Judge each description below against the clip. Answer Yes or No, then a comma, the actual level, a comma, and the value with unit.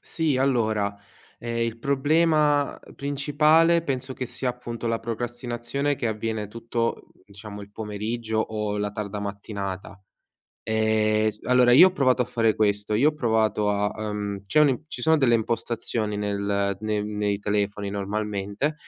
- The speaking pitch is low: Yes, low, 110 Hz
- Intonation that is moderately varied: Yes, average, 3.7 semitones